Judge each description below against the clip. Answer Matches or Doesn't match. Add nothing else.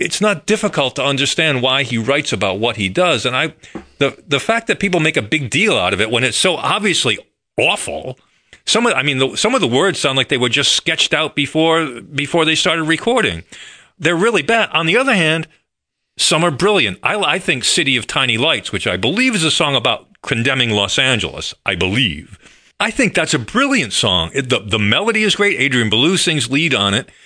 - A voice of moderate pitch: Matches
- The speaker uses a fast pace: Matches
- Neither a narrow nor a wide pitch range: Matches